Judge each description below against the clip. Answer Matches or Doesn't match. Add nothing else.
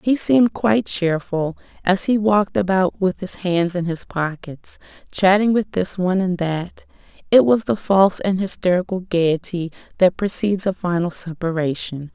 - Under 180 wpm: Matches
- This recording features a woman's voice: Matches